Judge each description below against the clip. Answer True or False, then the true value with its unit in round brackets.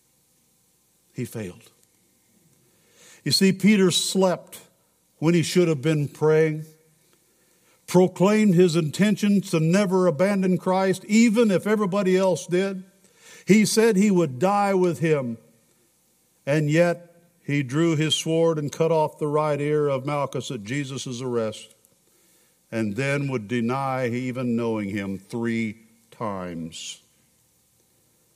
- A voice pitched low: False (160 Hz)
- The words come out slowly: True (120 wpm)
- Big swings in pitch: True (6.3 semitones)